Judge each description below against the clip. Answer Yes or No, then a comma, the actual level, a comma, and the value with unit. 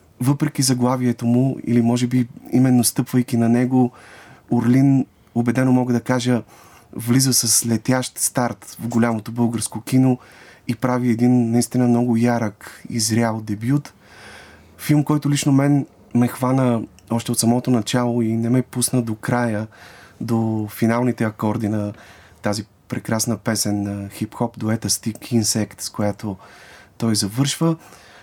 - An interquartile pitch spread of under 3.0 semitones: Yes, narrow, 2.4 semitones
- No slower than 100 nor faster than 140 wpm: Yes, average, 135 wpm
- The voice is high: No, low, 120 Hz